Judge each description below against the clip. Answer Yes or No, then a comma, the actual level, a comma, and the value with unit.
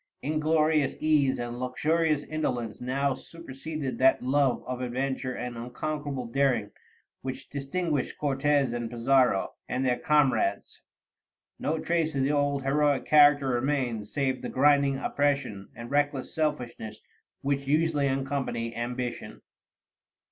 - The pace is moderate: No, slow, 120 wpm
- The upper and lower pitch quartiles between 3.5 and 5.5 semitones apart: No, average, 2.8 semitones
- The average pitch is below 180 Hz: Yes, low, 135 Hz